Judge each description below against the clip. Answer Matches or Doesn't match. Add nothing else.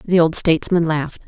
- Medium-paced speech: Matches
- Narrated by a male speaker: Doesn't match